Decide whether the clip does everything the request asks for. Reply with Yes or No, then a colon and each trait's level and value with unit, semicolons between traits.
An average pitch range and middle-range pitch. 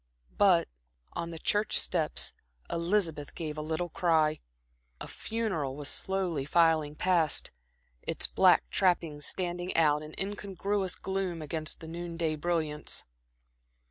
Yes: average, 3.0 semitones; medium, 165 Hz